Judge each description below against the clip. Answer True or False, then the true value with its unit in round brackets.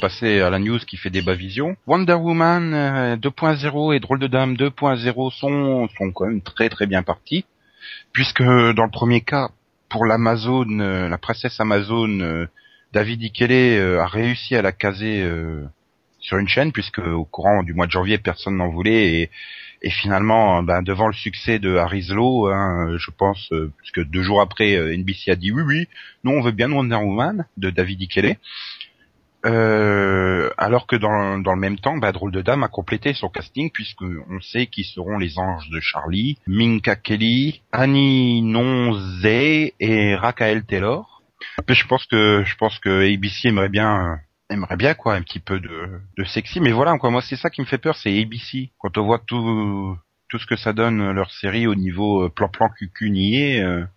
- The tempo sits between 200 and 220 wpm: False (180 wpm)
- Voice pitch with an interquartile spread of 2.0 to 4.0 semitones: False (4.5 semitones)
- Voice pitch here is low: True (110 Hz)